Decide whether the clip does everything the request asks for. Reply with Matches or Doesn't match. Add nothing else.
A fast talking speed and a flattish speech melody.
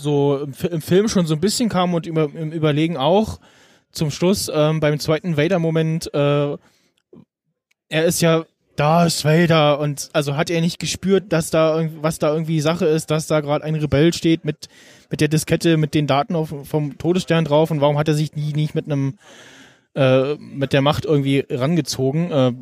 Matches